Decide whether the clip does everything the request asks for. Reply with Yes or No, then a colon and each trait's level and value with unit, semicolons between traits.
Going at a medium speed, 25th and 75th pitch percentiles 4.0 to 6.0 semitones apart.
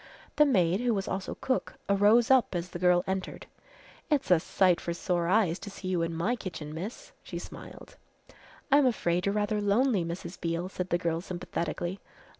No: average, 185 wpm; average, 3.4 semitones